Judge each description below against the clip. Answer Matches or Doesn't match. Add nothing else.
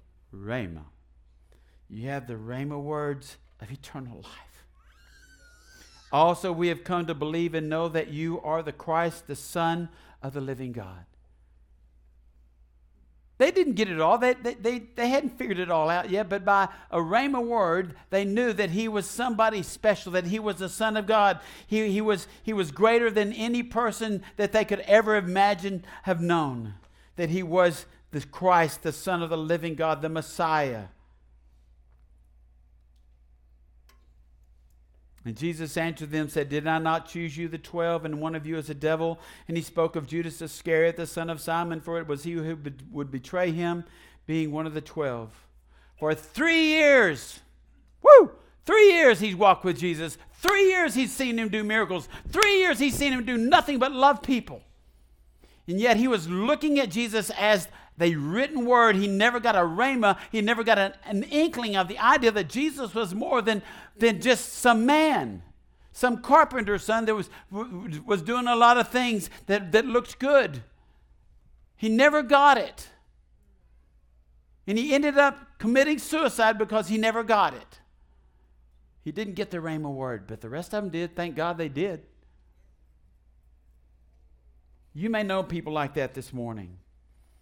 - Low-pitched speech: Doesn't match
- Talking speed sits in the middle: Matches